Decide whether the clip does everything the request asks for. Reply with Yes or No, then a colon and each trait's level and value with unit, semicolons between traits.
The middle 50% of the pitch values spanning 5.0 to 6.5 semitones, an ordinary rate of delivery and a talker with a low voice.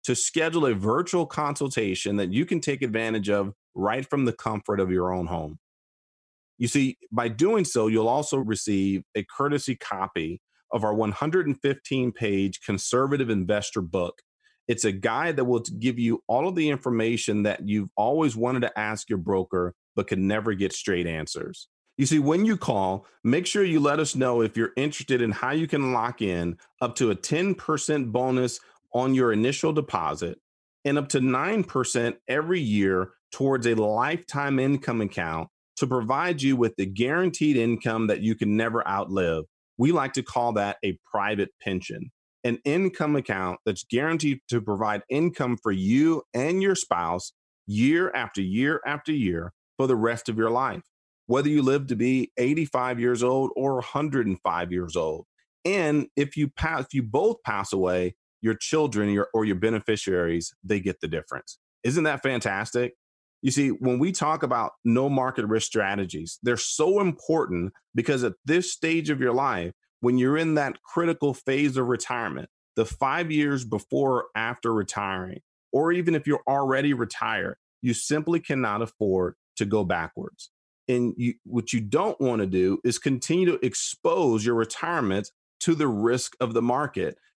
Yes: wide, 5.4 semitones; average, 170 wpm; low, 120 Hz